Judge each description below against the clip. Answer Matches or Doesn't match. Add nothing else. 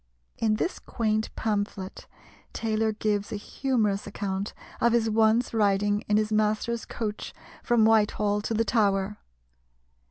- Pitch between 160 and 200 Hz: Doesn't match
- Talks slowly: Matches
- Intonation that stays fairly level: Matches